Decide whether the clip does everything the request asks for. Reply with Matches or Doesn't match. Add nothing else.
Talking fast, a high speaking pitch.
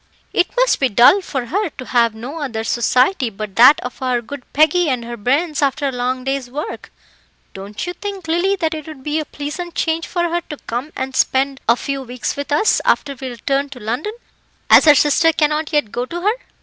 Matches